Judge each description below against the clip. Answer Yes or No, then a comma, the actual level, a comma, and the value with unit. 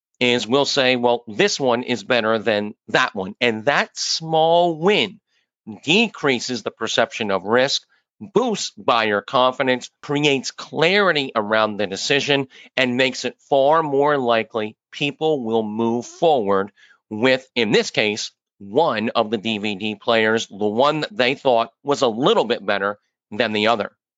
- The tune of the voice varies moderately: Yes, average, 4.3 semitones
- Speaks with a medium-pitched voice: No, low, 125 Hz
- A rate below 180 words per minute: Yes, average, 150 wpm